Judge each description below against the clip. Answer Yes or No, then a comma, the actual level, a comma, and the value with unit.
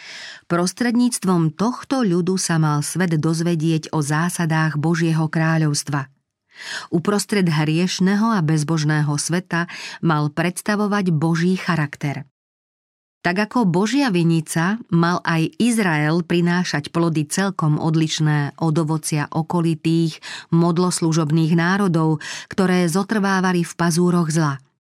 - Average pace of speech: No, slow, 100 wpm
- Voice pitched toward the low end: No, medium, 170 Hz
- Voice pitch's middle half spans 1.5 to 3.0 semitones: Yes, narrow, 2.6 semitones